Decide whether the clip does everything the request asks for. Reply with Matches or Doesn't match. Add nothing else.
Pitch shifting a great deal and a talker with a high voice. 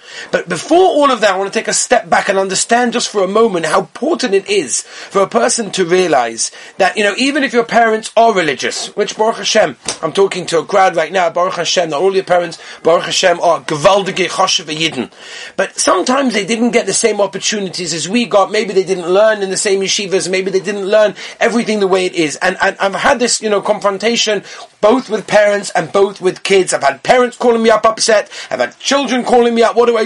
Doesn't match